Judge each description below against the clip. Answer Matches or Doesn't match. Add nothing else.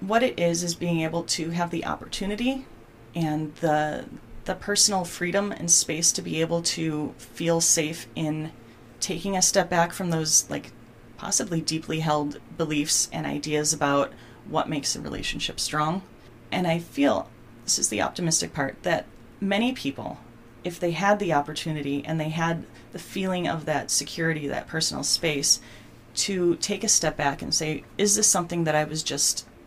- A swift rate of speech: Doesn't match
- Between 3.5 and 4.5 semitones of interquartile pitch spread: Doesn't match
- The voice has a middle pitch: Matches